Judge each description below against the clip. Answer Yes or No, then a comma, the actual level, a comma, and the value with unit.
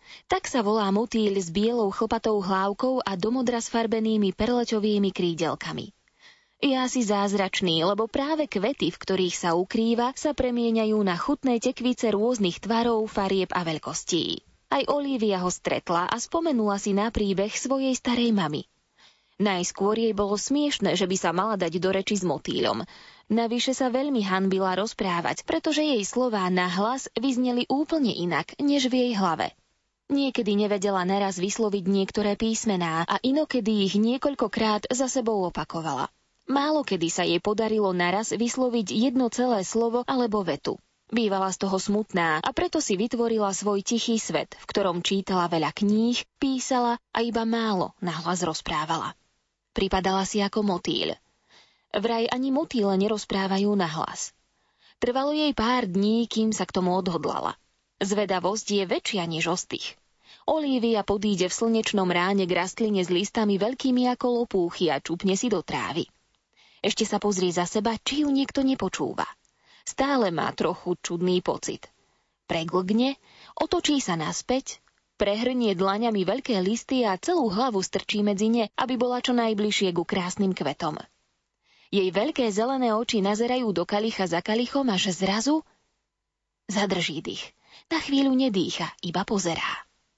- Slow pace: No, average, 145 wpm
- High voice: Yes, high, 215 Hz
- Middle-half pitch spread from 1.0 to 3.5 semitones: No, average, 4.4 semitones